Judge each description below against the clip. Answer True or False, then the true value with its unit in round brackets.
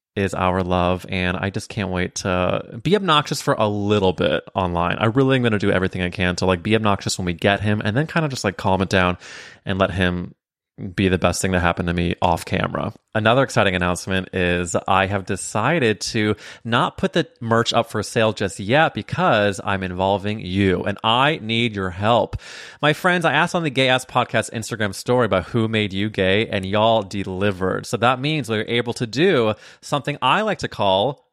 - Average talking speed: False (215 wpm)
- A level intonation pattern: False (4.3 semitones)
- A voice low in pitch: True (105 Hz)